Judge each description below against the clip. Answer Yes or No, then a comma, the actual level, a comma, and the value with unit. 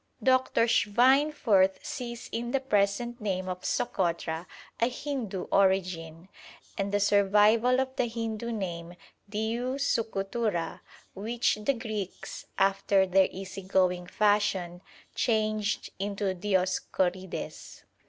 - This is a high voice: Yes, high, 205 Hz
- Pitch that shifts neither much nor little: Yes, average, 3.7 semitones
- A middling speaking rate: No, slow, 105 wpm